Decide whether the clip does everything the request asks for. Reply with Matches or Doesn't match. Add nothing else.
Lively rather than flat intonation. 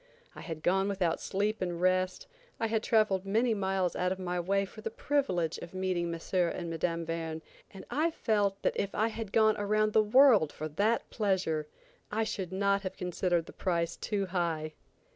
Doesn't match